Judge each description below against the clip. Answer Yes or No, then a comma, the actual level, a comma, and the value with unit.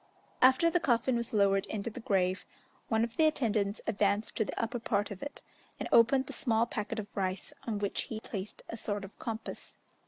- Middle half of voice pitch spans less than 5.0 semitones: Yes, average, 2.7 semitones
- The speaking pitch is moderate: No, high, 220 Hz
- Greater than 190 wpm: Yes, average, 200 wpm